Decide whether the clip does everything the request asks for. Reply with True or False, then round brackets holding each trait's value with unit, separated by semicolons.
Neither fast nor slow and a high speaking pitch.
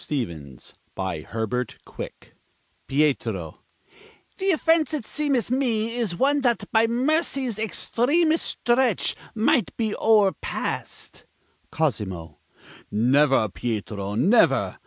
False (95 wpm; 215 Hz)